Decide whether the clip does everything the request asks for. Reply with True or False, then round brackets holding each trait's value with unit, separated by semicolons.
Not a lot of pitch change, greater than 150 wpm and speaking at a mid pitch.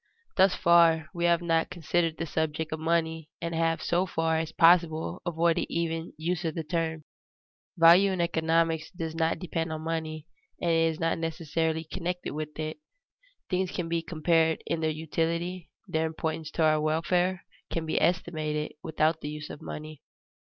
True (1.2 semitones; 170 wpm; 165 Hz)